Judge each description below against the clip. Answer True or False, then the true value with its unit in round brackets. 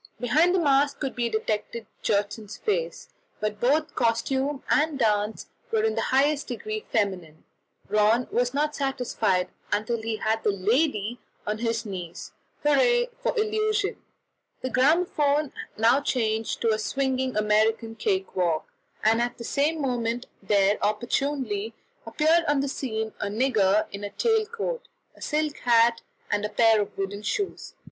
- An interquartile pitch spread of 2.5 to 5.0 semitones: False (5.4 semitones)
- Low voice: False (235 Hz)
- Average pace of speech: True (150 wpm)